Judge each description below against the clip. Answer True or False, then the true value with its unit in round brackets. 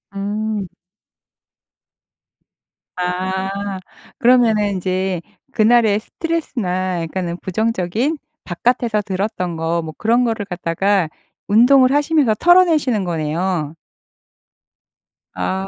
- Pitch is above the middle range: True (200 Hz)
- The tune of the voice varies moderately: True (4.7 semitones)